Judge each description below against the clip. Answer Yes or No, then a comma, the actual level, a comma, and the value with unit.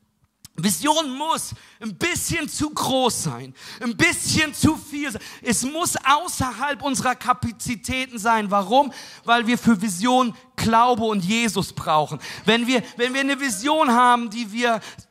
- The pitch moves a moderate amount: Yes, average, 3.5 semitones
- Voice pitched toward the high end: Yes, high, 245 Hz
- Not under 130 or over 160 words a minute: Yes, average, 140 wpm